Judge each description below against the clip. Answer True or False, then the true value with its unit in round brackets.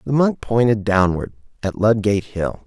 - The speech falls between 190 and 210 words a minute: False (160 wpm)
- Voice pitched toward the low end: True (105 Hz)